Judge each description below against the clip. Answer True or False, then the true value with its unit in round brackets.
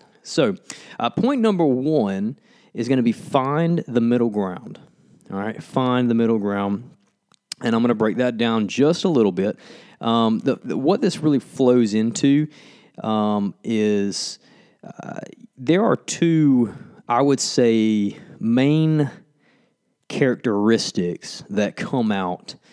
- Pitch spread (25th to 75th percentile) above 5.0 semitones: True (5.6 semitones)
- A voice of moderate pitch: False (125 Hz)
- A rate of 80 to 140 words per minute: True (135 wpm)